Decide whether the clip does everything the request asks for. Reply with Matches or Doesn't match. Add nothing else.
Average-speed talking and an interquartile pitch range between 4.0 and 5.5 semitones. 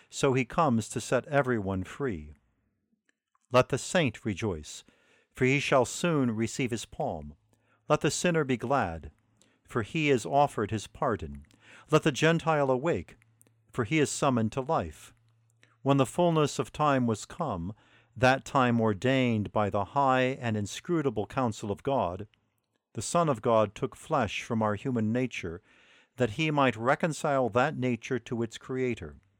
Matches